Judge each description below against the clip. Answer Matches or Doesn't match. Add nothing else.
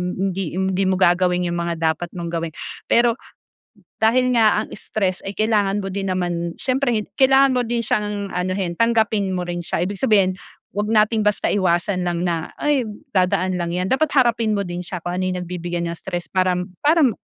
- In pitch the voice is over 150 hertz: Matches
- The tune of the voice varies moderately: Matches